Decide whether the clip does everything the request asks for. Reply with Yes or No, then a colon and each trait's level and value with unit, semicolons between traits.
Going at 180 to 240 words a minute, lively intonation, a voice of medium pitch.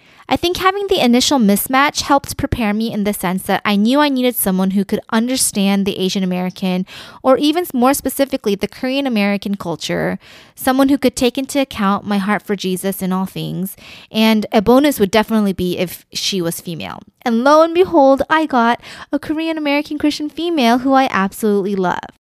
No: average, 190 wpm; wide, 5.9 semitones; high, 225 Hz